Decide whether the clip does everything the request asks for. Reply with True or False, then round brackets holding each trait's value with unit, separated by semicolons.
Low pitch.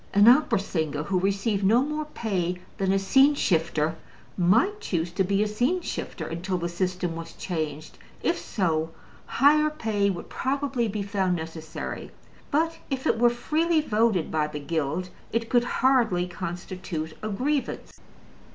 False (195 Hz)